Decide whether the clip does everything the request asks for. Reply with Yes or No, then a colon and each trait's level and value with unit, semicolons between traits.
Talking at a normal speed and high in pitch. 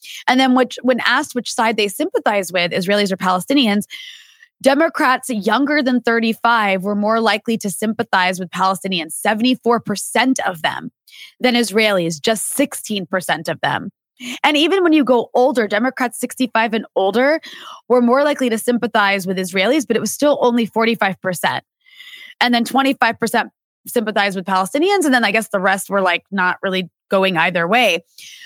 Yes: average, 160 wpm; high, 230 Hz